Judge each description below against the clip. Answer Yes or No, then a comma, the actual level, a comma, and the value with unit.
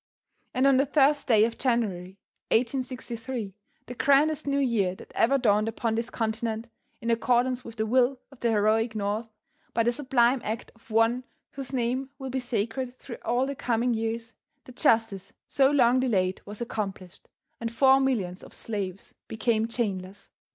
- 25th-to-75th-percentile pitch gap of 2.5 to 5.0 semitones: Yes, average, 2.8 semitones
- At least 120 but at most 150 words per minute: No, average, 165 wpm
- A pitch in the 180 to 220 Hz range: No, high, 235 Hz